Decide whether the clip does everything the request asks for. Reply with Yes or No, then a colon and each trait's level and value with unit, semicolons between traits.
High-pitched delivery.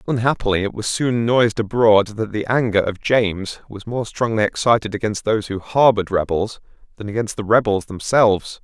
No: low, 110 Hz